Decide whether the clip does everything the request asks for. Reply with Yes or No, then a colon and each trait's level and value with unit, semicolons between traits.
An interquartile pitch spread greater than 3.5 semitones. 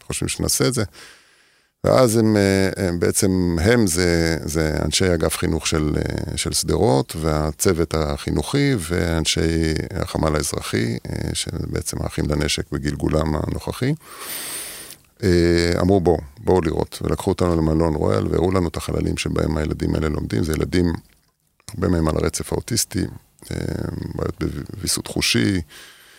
No: average, 3.0 semitones